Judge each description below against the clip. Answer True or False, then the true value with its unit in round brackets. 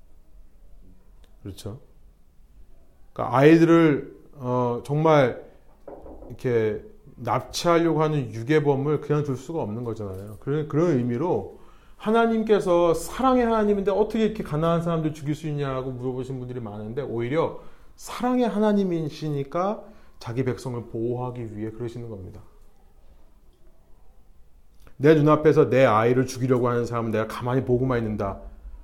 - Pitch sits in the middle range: False (130 Hz)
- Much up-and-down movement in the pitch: True (6.7 semitones)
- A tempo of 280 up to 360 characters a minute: True (310 characters per minute)